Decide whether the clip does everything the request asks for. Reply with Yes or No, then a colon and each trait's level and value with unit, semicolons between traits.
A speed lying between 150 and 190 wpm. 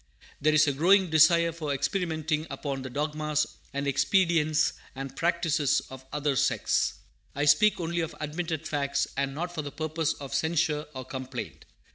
Yes: average, 160 wpm